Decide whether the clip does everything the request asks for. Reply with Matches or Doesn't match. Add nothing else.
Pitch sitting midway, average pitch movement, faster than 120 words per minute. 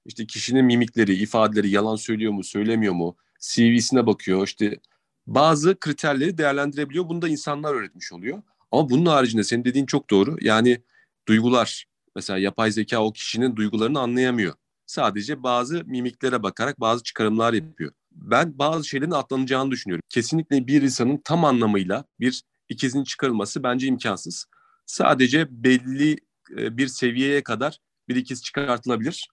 Doesn't match